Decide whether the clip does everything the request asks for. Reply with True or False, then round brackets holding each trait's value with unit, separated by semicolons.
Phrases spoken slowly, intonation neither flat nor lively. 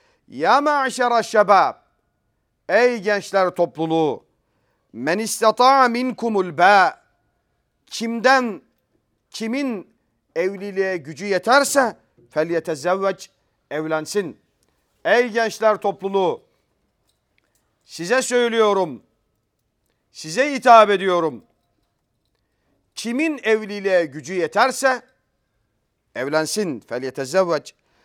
False (60 wpm; 6.9 semitones)